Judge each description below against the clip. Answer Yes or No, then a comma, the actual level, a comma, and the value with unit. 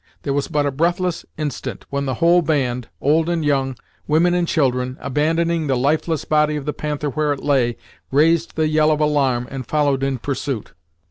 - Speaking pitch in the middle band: Yes, medium, 150 Hz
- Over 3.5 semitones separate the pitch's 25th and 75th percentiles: No, narrow, 2.6 semitones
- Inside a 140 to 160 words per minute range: No, average, 190 wpm